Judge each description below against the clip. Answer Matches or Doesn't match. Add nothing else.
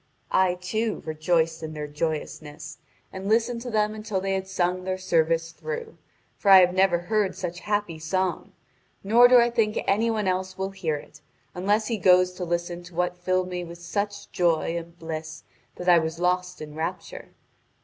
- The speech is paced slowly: Doesn't match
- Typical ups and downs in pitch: Matches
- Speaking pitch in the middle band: Matches